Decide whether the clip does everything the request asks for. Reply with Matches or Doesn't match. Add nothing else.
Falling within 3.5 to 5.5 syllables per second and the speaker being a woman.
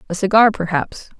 Matches